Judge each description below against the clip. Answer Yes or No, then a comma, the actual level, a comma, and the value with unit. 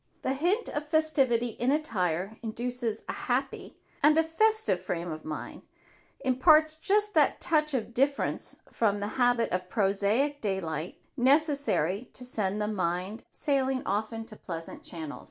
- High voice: Yes, high, 240 Hz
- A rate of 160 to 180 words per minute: No, average, 145 wpm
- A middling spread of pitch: No, wide, 6.8 semitones